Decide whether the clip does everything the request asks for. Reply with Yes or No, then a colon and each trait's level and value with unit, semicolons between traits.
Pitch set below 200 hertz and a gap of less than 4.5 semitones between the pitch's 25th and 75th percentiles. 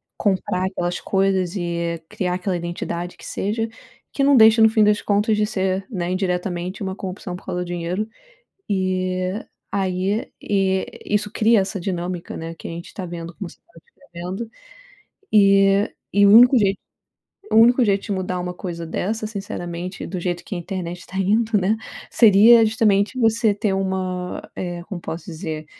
Yes: high, 190 Hz; average, 2.8 semitones